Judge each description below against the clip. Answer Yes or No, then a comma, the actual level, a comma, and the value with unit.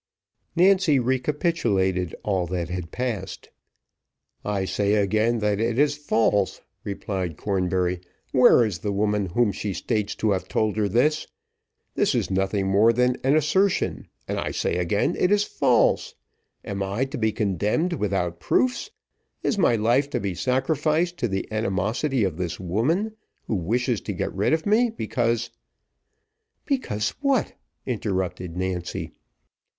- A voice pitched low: Yes, low, 110 Hz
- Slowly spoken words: No, average, 145 wpm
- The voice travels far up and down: Yes, wide, 6.5 semitones